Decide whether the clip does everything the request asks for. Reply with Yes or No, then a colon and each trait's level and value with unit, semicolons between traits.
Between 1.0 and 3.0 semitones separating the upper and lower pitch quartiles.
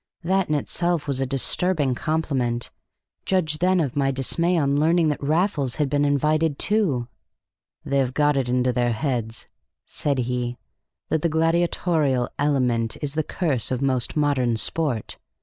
No: average, 4.0 semitones